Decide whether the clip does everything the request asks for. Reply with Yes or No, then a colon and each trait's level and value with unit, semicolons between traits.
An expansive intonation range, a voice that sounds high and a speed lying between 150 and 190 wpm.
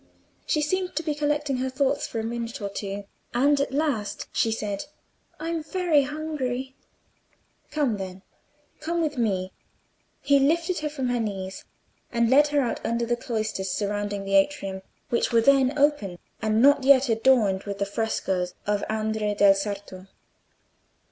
Yes: wide, 6.0 semitones; high, 235 Hz; average, 160 wpm